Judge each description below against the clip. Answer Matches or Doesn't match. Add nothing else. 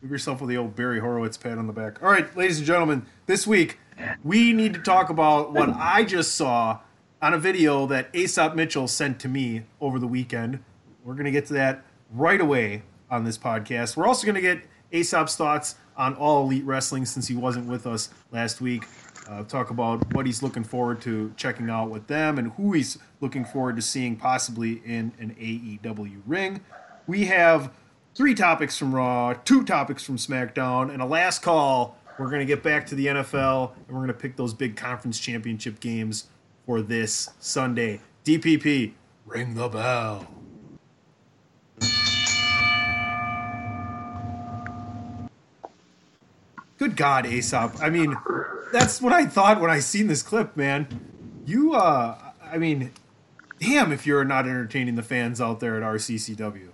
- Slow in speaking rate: Doesn't match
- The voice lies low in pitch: Matches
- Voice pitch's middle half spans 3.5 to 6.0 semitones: Matches